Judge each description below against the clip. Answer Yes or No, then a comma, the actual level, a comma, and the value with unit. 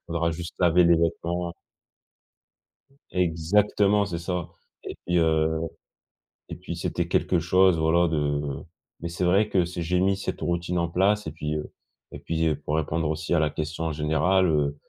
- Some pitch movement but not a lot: No, narrow, 2.1 semitones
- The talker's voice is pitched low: Yes, very low, 85 Hz